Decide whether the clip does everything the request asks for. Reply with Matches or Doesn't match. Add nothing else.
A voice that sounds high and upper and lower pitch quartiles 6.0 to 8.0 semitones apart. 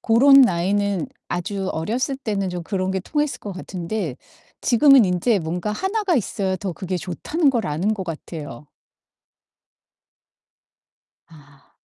Doesn't match